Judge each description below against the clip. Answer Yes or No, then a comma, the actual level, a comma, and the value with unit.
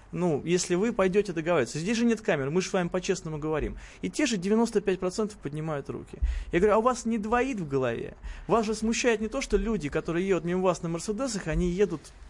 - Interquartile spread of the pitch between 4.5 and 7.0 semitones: Yes, average, 5.2 semitones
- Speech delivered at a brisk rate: Yes, fast, 220 wpm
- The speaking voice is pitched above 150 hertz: Yes, medium, 185 Hz